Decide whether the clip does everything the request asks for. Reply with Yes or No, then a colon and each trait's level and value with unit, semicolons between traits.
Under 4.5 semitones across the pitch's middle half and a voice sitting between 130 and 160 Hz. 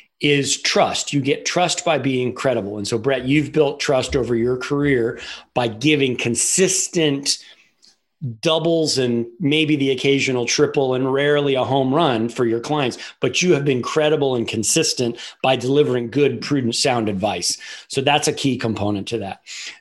Yes: average, 3.3 semitones; low, 135 Hz